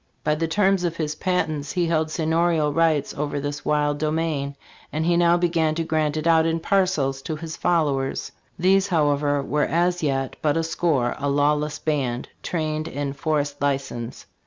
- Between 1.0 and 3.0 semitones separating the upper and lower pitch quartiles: Yes, narrow, 2.4 semitones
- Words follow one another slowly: No, average, 175 wpm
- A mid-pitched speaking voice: Yes, medium, 155 Hz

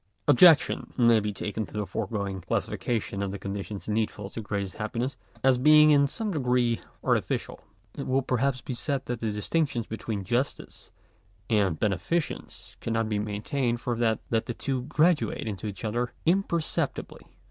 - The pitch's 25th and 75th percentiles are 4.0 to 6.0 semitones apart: Yes, average, 4.3 semitones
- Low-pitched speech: Yes, low, 115 Hz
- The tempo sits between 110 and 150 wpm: No, average, 160 wpm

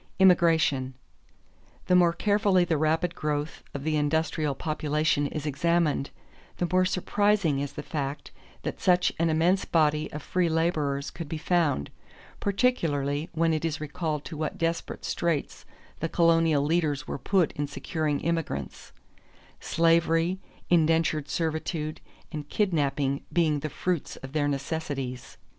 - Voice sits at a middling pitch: Yes, medium, 160 Hz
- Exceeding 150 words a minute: No, slow, 135 wpm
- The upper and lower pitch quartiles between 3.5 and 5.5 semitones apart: No, narrow, 2.6 semitones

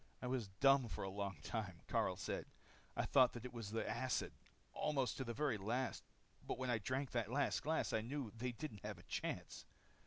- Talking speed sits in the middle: No, fast, 210 wpm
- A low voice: Yes, low, 120 Hz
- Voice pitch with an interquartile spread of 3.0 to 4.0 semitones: Yes, average, 3.6 semitones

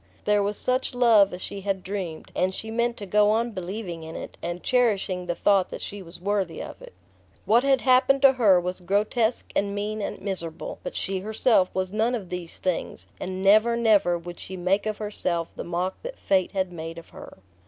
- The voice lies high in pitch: Yes, high, 200 Hz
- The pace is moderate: No, fast, 210 wpm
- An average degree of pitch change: Yes, average, 3.4 semitones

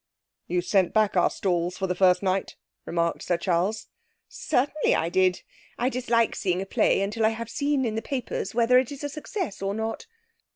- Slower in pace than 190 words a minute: No, average, 195 wpm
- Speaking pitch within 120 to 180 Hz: No, high, 210 Hz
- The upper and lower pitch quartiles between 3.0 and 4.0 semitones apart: No, average, 5.1 semitones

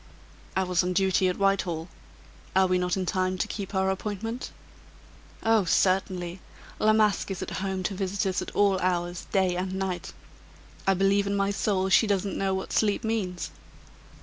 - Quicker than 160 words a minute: Yes, average, 175 wpm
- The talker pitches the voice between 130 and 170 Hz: No, high, 190 Hz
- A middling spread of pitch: No, narrow, 1.5 semitones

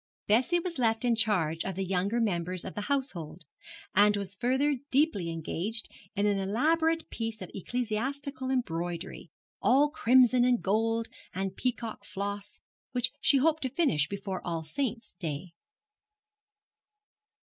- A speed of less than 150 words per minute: Yes, average, 140 wpm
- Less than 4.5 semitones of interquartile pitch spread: No, average, 5.3 semitones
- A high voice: Yes, high, 220 Hz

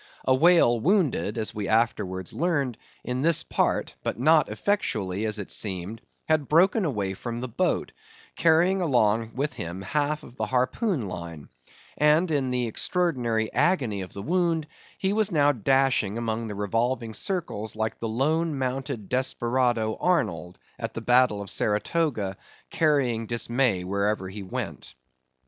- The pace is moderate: Yes, average, 150 wpm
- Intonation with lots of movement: Yes, wide, 6.2 semitones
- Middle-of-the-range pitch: No, low, 125 Hz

